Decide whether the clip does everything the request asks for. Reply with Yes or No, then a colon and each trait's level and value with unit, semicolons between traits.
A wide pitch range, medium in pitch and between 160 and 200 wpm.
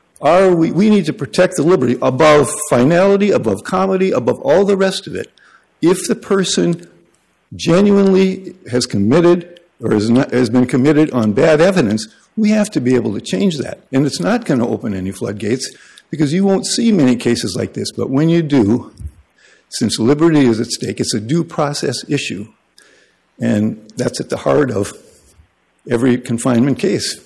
Yes: wide, 7.2 semitones; medium, 150 Hz; average, 175 wpm